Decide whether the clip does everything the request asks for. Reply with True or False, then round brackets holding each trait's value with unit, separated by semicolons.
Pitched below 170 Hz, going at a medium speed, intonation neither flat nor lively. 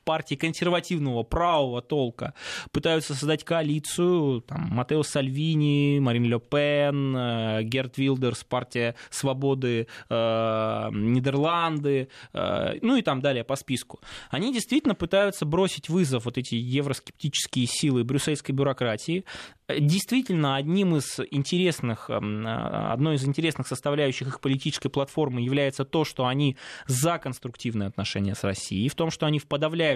True (140 Hz; 130 wpm; 4.1 semitones)